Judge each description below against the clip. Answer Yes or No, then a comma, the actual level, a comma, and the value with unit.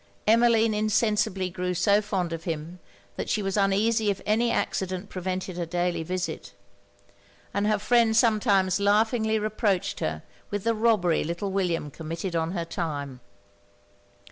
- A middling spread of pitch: Yes, average, 3.6 semitones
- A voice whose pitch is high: Yes, high, 195 Hz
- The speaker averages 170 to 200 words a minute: No, average, 140 wpm